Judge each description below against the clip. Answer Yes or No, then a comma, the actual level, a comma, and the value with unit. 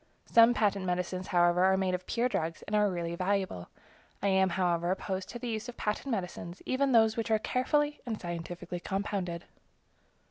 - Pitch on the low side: No, high, 190 Hz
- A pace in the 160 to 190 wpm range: Yes, average, 185 wpm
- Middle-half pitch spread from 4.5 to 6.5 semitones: No, average, 3.9 semitones